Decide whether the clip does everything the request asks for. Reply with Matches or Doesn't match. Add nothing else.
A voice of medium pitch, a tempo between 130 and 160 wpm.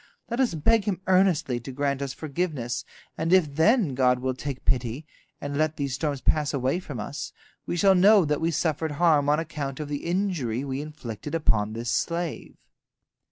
Doesn't match